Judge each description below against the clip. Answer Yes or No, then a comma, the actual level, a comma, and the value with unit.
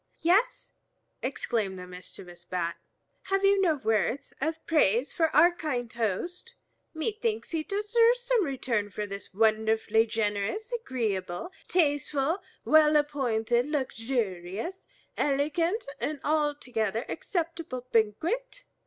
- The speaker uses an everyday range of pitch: No, wide, 7.8 semitones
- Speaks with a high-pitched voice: Yes, very high, 275 Hz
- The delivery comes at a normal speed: No, slow, 110 wpm